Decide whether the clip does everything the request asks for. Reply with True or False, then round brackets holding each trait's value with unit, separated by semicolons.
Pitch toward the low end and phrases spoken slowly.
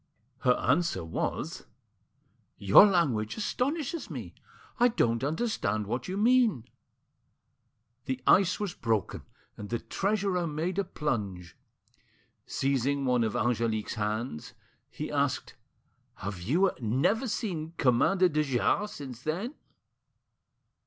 False (145 Hz; 110 wpm)